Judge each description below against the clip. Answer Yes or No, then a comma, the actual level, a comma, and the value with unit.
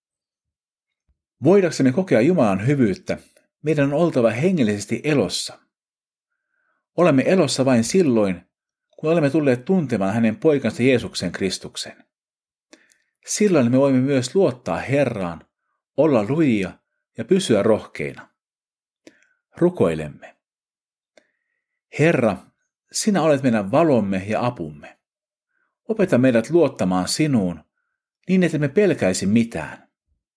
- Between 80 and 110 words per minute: Yes, slow, 95 wpm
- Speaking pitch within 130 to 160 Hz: Yes, medium, 140 Hz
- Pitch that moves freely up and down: Yes, wide, 8.7 semitones